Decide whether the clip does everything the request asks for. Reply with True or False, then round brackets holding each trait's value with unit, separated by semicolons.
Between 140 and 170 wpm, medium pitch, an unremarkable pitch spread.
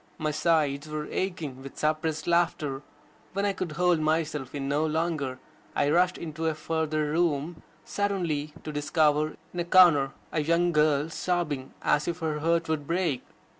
False (165 wpm; 155 Hz; 2.3 semitones)